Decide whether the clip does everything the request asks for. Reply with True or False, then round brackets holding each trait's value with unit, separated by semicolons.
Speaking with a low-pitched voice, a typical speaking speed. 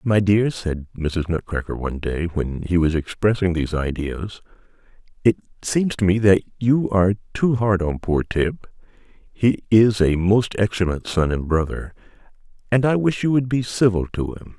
True (100 Hz; 175 wpm)